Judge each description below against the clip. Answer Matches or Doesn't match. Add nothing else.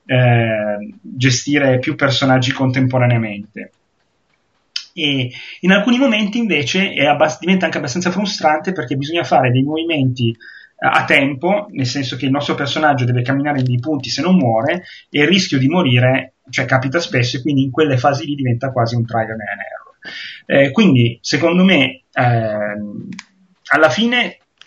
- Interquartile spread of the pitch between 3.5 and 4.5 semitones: Matches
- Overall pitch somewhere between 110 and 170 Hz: Matches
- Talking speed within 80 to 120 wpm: Doesn't match